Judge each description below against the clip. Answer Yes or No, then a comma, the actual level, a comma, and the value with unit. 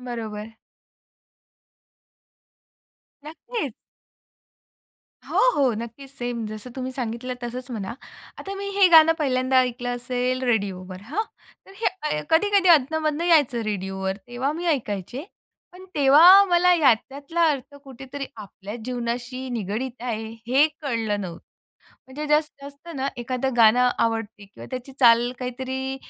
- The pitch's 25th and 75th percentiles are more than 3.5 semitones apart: Yes, average, 4.0 semitones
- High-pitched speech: Yes, very high, 255 Hz